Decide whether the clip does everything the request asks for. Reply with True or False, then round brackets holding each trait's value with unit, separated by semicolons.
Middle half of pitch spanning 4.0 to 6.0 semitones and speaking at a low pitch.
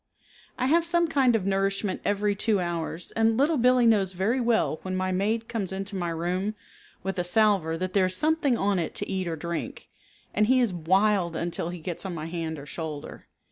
False (4.4 semitones; 195 Hz)